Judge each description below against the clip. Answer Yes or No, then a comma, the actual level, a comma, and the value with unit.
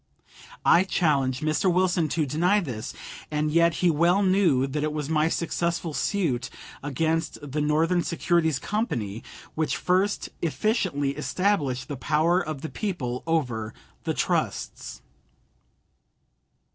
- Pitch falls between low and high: Yes, medium, 160 Hz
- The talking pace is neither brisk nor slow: No, slow, 125 wpm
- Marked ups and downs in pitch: No, average, 3.7 semitones